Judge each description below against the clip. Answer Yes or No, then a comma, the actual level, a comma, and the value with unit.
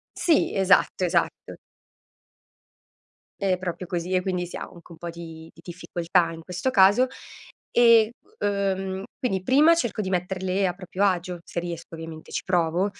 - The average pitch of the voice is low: No, medium, 185 Hz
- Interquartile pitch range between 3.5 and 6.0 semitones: No, narrow, 2.4 semitones